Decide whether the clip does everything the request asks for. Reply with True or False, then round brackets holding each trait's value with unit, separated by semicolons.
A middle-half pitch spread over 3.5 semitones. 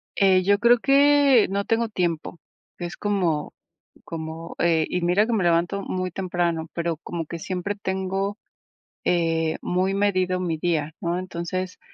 False (2.9 semitones)